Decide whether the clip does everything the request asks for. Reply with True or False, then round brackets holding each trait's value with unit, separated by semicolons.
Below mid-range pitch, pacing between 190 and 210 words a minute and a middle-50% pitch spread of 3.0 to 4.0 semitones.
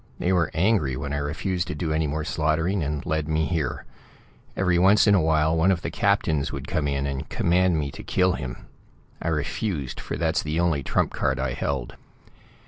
True (80 Hz; 205 wpm; 3.5 semitones)